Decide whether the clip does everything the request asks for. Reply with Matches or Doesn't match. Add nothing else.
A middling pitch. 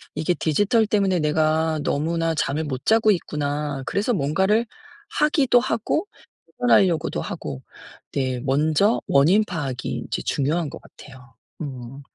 Matches